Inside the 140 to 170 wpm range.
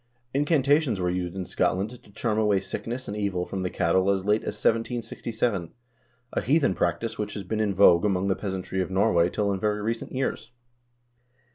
No: average, 190 wpm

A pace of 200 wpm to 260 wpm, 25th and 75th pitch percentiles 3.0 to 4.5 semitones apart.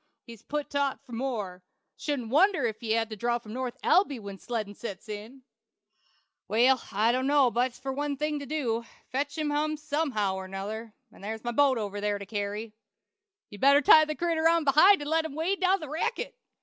No: fast, 205 wpm; average, 5.3 semitones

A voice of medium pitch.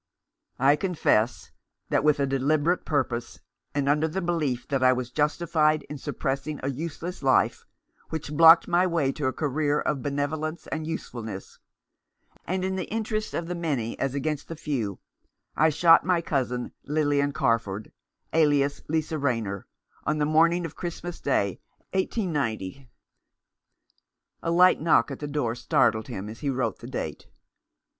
Yes: medium, 150 Hz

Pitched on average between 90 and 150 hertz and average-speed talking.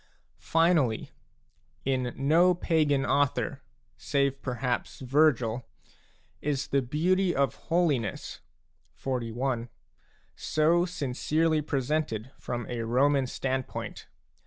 No: medium, 140 Hz; slow, 85 wpm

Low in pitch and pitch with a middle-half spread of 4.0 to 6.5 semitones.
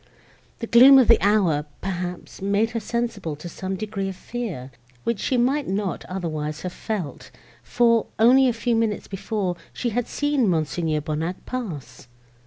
No: high, 205 Hz; average, 4.9 semitones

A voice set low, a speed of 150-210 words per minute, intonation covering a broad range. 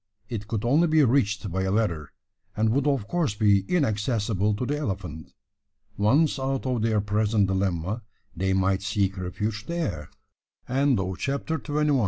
Yes: low, 110 Hz; average, 160 wpm; wide, 5.7 semitones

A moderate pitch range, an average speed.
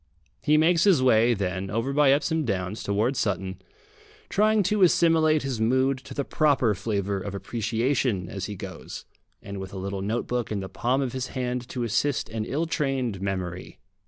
No: wide, 5.8 semitones; average, 180 wpm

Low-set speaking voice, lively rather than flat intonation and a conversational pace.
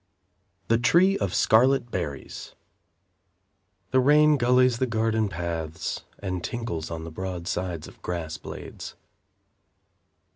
No: low, 105 Hz; wide, 6.7 semitones; slow, 115 wpm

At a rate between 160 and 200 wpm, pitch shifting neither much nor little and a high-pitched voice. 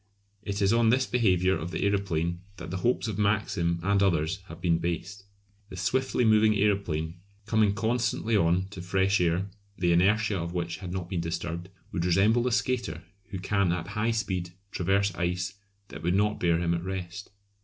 No: average, 185 wpm; average, 3.2 semitones; very low, 95 Hz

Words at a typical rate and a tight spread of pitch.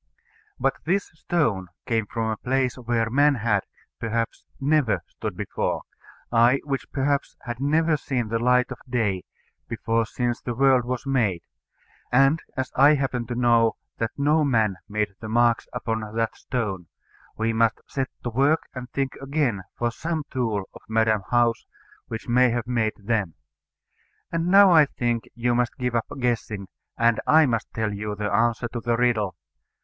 No: average, 165 wpm; average, 3.2 semitones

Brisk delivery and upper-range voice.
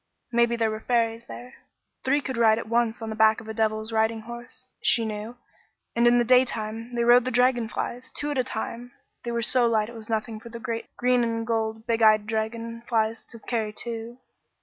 Yes: fast, 215 wpm; high, 230 Hz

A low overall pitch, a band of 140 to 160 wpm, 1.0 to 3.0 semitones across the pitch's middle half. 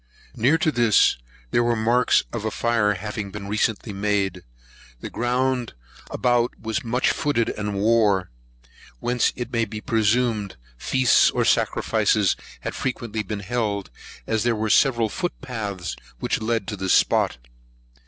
Yes: low, 110 Hz; average, 145 wpm; average, 2.7 semitones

